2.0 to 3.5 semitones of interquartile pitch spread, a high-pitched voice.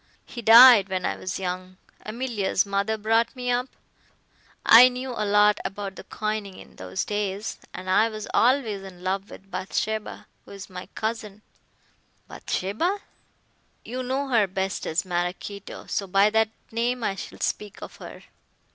Yes: average, 3.1 semitones; high, 210 Hz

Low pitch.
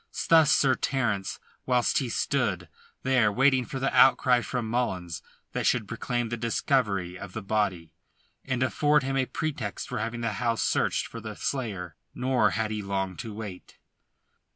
Yes: low, 115 Hz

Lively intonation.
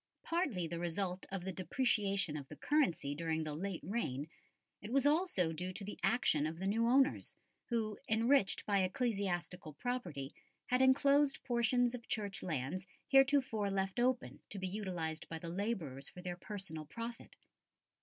Yes: wide, 6.1 semitones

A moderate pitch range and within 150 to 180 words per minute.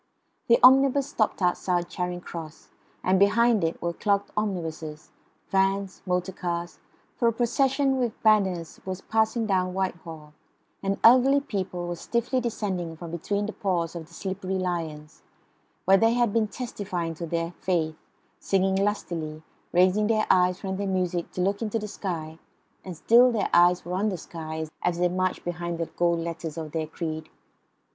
Yes: average, 3.7 semitones; average, 165 wpm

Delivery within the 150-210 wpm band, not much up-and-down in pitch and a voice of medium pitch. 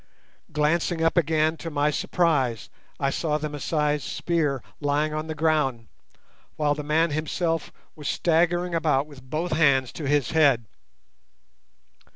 No: average, 140 wpm; narrow, 2.2 semitones; medium, 150 Hz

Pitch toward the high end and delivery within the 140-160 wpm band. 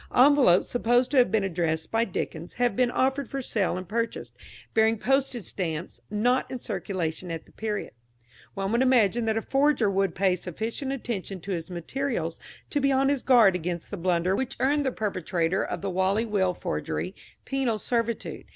No: high, 220 Hz; average, 180 wpm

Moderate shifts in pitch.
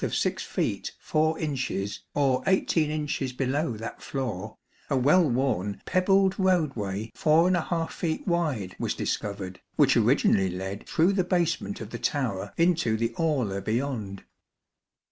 No: wide, 7.6 semitones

